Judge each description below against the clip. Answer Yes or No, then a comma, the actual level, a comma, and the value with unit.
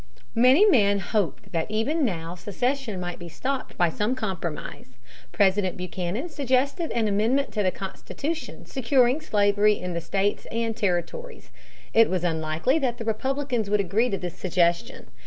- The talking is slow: No, average, 155 wpm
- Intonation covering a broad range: Yes, wide, 6.1 semitones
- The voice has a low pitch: No, high, 210 Hz